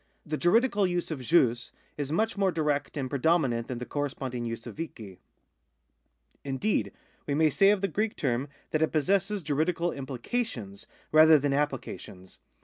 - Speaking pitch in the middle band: Yes, medium, 150 Hz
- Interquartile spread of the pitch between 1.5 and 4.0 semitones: No, average, 5.3 semitones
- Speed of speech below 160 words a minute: No, average, 165 wpm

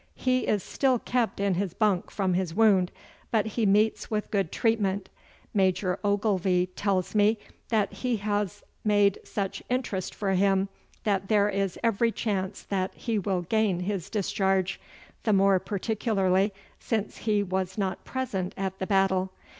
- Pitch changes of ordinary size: No, narrow, 2.1 semitones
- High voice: Yes, high, 200 Hz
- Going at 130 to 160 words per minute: Yes, average, 155 wpm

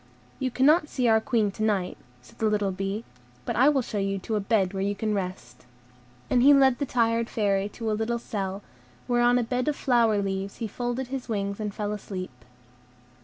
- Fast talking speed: Yes, fast, 215 wpm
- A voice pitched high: Yes, high, 220 Hz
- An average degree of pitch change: Yes, average, 3.6 semitones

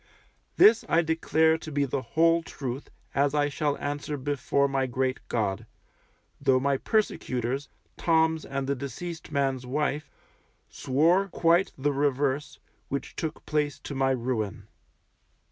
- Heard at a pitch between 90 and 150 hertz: Yes, medium, 140 Hz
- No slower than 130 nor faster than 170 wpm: Yes, slow, 135 wpm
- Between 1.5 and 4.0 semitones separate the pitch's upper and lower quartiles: Yes, average, 3.2 semitones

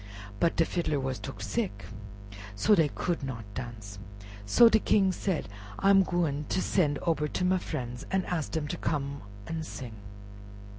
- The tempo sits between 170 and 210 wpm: Yes, average, 175 wpm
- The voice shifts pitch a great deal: Yes, wide, 5.9 semitones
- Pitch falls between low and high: Yes, medium, 150 Hz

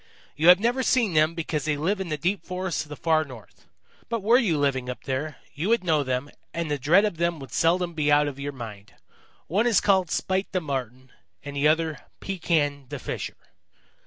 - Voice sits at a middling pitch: Yes, medium, 155 Hz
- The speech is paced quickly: Yes, fast, 215 wpm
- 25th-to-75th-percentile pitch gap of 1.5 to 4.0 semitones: No, average, 4.5 semitones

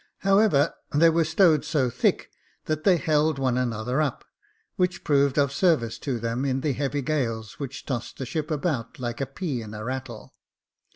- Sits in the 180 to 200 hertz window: No, medium, 140 Hz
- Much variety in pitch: No, average, 3.8 semitones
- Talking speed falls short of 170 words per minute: No, average, 180 wpm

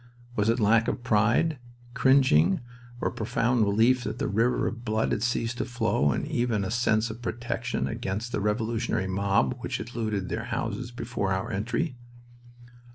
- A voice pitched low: Yes, low, 115 Hz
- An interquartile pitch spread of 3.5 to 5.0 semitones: No, average, 2.7 semitones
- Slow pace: No, average, 170 wpm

